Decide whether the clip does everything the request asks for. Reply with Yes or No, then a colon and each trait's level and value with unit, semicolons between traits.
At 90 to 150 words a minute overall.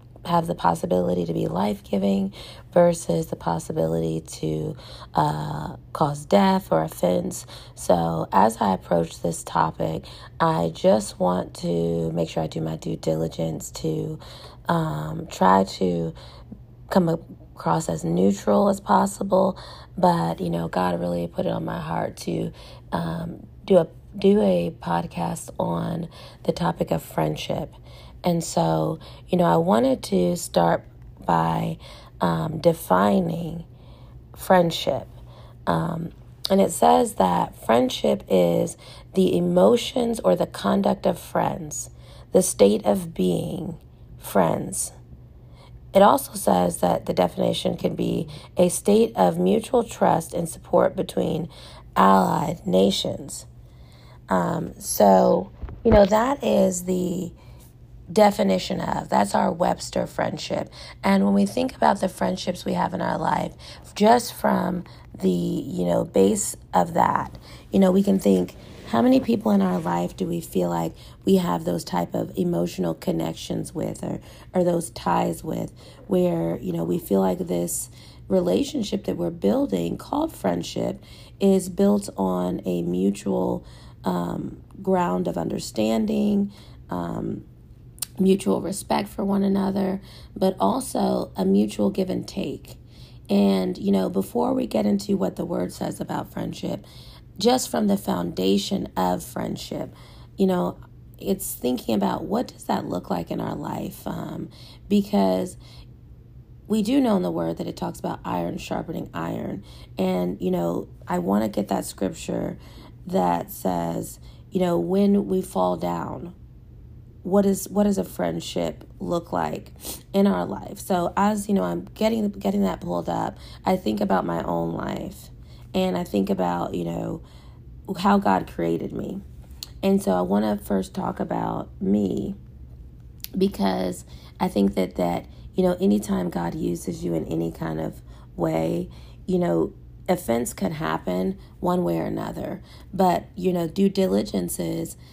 Yes: average, 145 wpm